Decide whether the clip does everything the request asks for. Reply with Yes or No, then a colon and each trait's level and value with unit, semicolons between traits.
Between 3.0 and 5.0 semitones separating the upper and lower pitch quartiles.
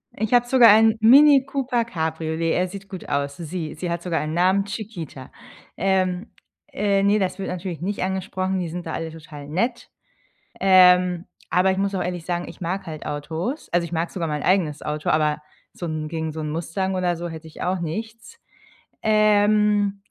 Yes: average, 3.7 semitones